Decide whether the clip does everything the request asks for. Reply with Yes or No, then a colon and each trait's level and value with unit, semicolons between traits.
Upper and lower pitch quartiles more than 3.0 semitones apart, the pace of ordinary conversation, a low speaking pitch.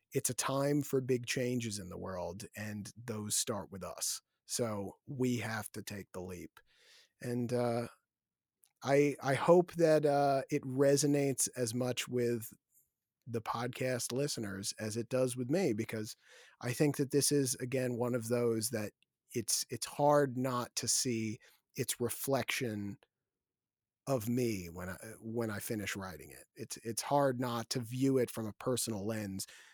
Yes: average, 3.7 semitones; average, 160 wpm; low, 120 Hz